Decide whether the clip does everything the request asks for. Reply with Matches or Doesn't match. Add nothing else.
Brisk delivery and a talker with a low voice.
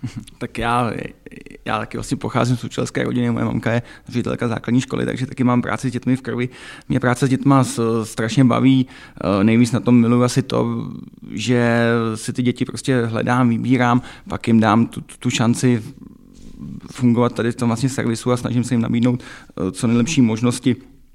Matches